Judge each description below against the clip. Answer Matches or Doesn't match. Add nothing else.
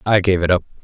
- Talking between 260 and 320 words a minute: Matches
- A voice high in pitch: Doesn't match